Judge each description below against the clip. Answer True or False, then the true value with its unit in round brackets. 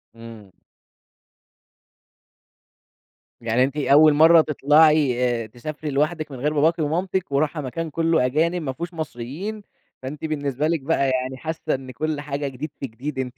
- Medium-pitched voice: True (150 Hz)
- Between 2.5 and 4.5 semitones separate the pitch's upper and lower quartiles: True (3.3 semitones)